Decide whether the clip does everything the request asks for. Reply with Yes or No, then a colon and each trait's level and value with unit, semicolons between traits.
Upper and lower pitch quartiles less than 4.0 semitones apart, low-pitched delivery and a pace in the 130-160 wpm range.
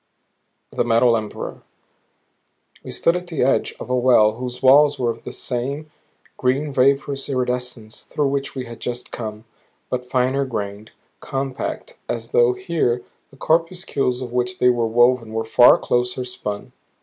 Yes: narrow, 2.4 semitones; low, 125 Hz; average, 155 wpm